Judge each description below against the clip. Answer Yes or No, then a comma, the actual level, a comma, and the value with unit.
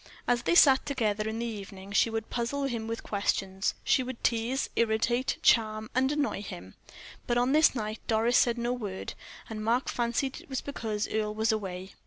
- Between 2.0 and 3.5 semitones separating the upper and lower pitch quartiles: Yes, narrow, 2.5 semitones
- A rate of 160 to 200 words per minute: Yes, average, 190 wpm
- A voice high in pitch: Yes, high, 230 Hz